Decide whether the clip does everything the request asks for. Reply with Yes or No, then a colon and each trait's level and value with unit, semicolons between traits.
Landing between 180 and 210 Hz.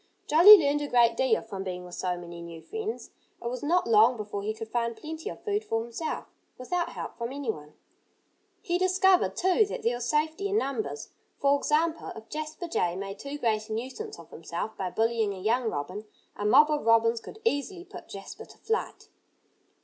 No: high, 245 Hz